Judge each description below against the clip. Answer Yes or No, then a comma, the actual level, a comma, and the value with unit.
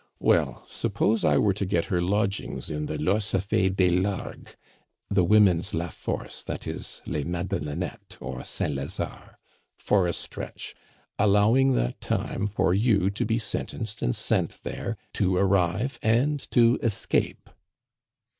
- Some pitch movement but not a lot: Yes, average, 3.5 semitones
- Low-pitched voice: Yes, very low, 95 Hz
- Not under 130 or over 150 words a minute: Yes, average, 140 wpm